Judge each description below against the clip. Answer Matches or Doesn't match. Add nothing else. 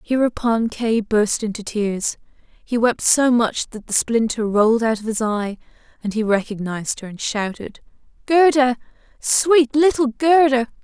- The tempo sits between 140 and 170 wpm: Matches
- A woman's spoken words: Matches